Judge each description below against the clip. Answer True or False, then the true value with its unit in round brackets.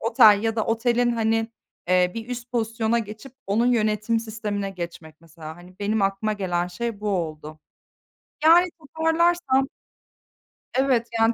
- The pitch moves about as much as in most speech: True (3.5 semitones)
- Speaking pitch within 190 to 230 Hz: True (220 Hz)